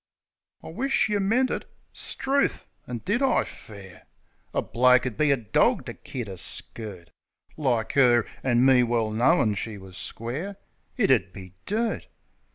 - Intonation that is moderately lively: No, wide, 9.0 semitones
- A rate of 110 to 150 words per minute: No, average, 160 wpm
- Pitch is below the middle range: Yes, low, 125 Hz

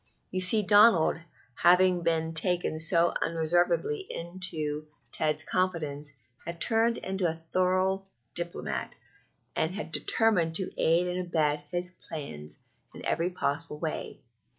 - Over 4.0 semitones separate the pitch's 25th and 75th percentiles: No, narrow, 2.6 semitones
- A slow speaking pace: Yes, slow, 125 wpm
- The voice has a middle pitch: Yes, medium, 175 Hz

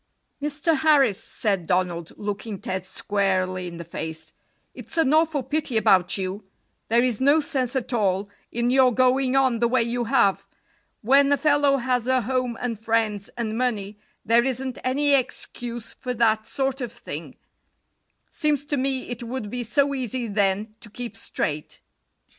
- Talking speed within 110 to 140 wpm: No, average, 165 wpm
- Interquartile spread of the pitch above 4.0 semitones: Yes, average, 4.4 semitones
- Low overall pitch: No, high, 240 Hz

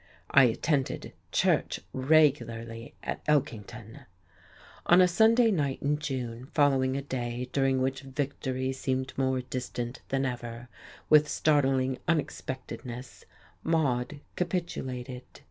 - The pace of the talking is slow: Yes, slow, 110 wpm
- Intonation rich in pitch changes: No, average, 2.8 semitones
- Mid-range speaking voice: No, low, 130 Hz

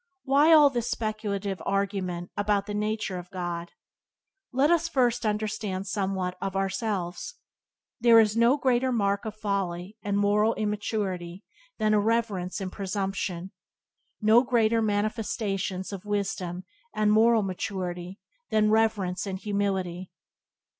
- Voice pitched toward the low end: No, high, 205 Hz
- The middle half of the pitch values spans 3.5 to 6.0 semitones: No, narrow, 2.5 semitones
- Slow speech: Yes, slow, 125 wpm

